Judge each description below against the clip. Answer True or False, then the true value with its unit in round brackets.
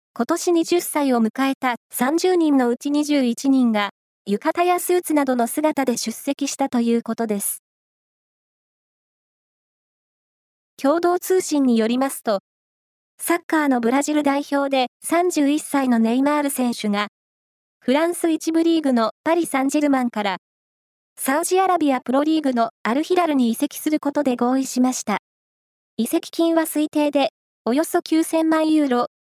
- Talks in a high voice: True (280 Hz)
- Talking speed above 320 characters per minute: False (275 characters per minute)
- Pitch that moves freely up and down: False (4.6 semitones)